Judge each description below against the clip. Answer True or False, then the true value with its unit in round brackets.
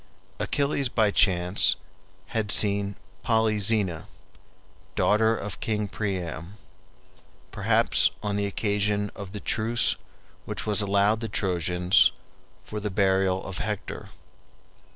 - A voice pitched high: False (100 Hz)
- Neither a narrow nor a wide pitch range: False (2.0 semitones)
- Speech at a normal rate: False (110 wpm)